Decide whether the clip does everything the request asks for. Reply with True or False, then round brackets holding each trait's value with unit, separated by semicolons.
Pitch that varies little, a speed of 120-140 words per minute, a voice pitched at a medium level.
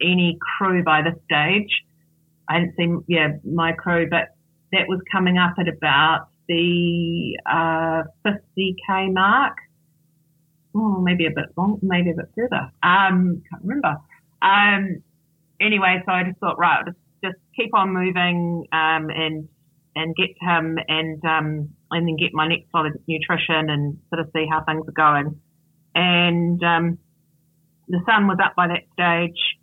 False (2.2 semitones; 160 wpm; 170 Hz)